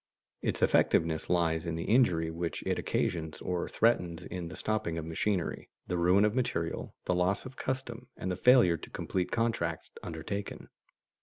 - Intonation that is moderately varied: Yes, average, 4.5 semitones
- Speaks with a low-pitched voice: Yes, very low, 90 Hz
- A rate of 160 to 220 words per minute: Yes, average, 165 wpm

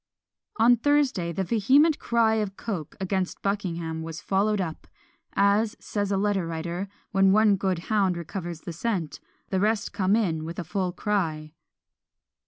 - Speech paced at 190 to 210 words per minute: No, average, 155 wpm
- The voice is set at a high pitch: Yes, high, 195 Hz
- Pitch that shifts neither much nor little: Yes, average, 3.7 semitones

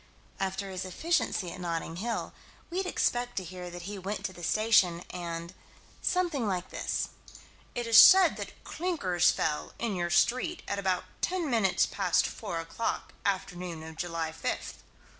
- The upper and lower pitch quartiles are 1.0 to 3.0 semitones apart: No, average, 5.2 semitones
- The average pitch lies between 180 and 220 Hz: Yes, high, 190 Hz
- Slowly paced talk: No, average, 160 wpm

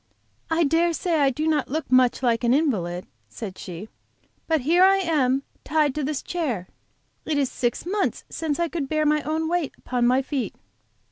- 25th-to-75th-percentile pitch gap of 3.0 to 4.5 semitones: Yes, average, 4.2 semitones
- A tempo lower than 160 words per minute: No, average, 190 wpm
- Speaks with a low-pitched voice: No, very high, 295 Hz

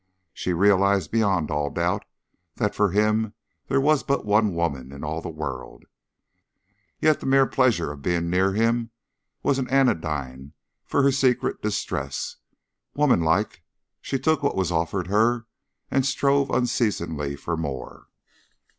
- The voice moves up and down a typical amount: No, wide, 7.7 semitones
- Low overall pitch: Yes, low, 100 Hz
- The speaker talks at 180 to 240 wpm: No, average, 140 wpm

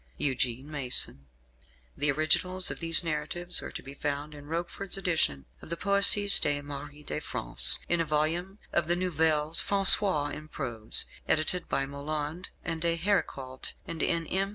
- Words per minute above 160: No, average, 155 wpm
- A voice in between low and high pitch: Yes, medium, 155 Hz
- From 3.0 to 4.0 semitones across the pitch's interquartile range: Yes, average, 3.4 semitones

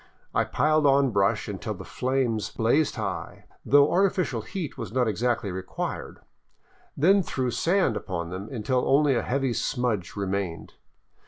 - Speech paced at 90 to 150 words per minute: Yes, average, 145 wpm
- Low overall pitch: Yes, low, 125 Hz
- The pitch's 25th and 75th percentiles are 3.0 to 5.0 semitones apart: No, wide, 5.5 semitones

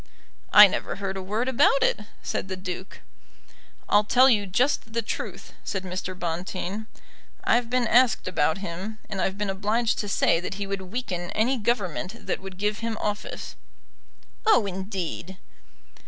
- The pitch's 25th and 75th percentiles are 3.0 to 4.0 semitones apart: Yes, average, 3.3 semitones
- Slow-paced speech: No, average, 160 wpm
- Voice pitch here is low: No, high, 200 Hz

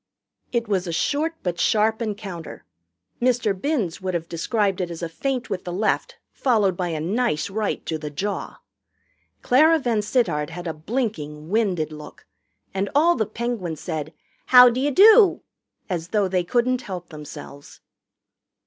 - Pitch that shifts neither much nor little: No, wide, 6.1 semitones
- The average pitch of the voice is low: No, high, 200 Hz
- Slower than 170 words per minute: Yes, average, 155 wpm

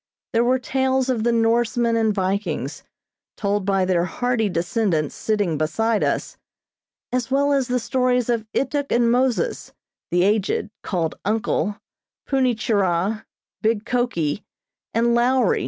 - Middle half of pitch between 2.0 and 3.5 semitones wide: No, average, 4.0 semitones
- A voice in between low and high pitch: No, high, 225 Hz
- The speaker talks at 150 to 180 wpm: No, slow, 135 wpm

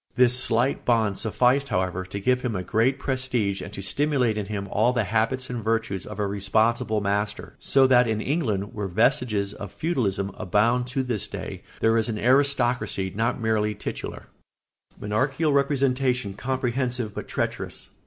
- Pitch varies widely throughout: No, average, 3.7 semitones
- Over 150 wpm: Yes, average, 165 wpm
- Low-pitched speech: Yes, low, 115 Hz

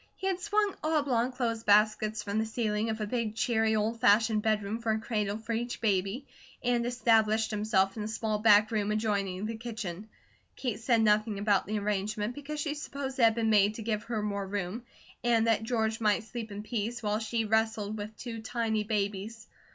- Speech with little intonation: Yes, narrow, 1.7 semitones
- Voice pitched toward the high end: Yes, high, 220 Hz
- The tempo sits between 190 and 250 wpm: Yes, average, 195 wpm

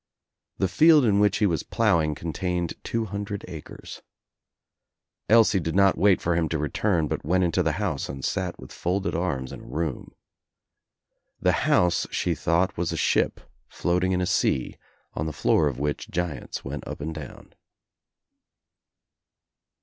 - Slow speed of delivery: No, average, 160 wpm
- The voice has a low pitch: Yes, very low, 85 Hz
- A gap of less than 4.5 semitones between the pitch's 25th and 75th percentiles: Yes, average, 3.9 semitones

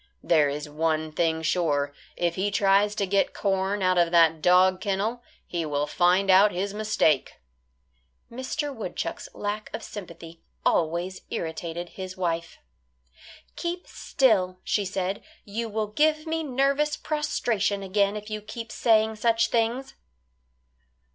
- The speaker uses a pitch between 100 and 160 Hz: No, high, 195 Hz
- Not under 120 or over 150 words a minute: Yes, slow, 135 wpm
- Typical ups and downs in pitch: Yes, average, 4.3 semitones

